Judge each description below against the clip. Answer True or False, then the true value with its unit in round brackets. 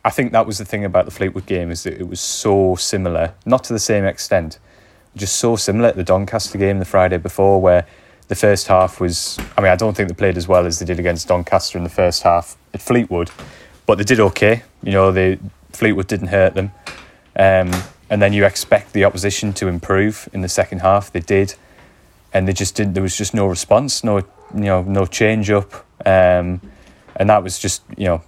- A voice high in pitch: False (95 Hz)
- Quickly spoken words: True (220 wpm)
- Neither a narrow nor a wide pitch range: False (2.2 semitones)